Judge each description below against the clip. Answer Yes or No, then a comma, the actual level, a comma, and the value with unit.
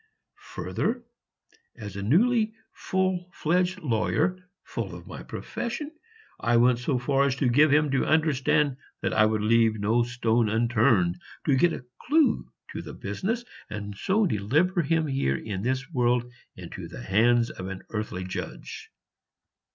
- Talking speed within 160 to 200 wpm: No, average, 150 wpm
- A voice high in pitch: No, low, 125 Hz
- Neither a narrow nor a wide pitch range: No, wide, 7.3 semitones